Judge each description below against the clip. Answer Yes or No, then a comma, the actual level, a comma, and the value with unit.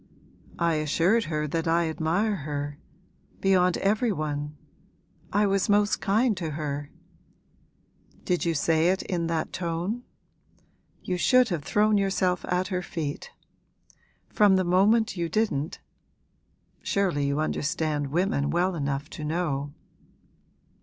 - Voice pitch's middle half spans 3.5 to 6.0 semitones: Yes, average, 4.3 semitones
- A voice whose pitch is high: No, medium, 170 Hz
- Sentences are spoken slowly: Yes, slow, 125 wpm